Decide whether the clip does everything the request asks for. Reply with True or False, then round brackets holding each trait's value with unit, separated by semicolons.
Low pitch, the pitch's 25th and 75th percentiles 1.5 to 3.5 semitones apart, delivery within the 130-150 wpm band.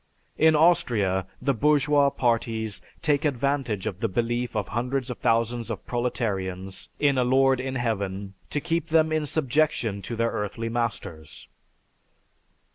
False (120 Hz; 4.5 semitones; 140 wpm)